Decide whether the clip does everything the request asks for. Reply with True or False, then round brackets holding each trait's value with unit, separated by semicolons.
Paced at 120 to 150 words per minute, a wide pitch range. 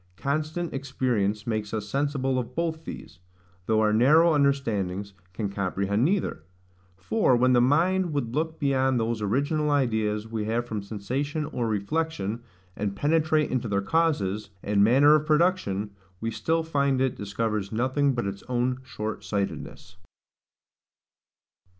True (140 wpm; 5.7 semitones)